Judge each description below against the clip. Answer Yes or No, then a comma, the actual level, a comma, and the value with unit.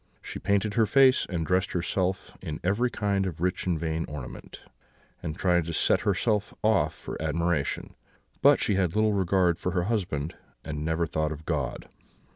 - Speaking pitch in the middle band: No, very low, 90 Hz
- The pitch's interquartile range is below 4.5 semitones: Yes, average, 3.9 semitones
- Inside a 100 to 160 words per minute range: No, average, 175 wpm